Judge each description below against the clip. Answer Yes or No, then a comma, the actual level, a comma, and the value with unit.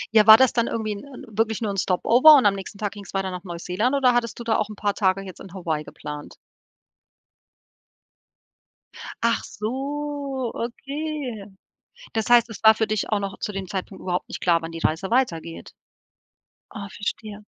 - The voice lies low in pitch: No, high, 215 Hz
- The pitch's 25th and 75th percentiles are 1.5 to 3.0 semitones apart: No, average, 3.9 semitones